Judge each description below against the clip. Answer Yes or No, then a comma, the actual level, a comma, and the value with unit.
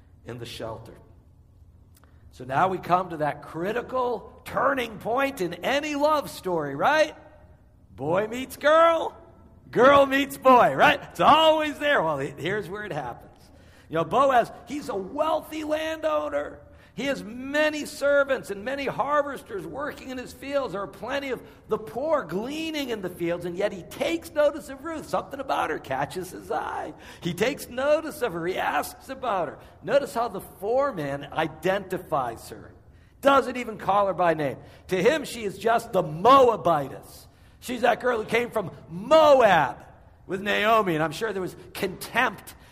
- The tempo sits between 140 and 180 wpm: Yes, average, 165 wpm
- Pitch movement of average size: No, wide, 8.7 semitones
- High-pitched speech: Yes, high, 225 Hz